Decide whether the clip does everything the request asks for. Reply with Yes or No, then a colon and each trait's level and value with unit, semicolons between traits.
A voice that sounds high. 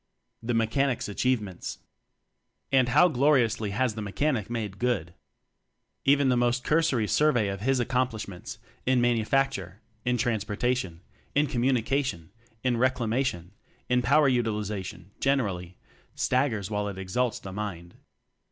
No: low, 120 Hz